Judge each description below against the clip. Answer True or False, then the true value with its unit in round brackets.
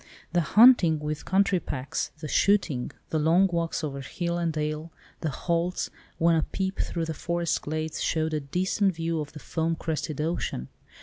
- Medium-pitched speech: True (165 Hz)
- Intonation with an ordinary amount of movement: False (2.2 semitones)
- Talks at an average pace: True (170 wpm)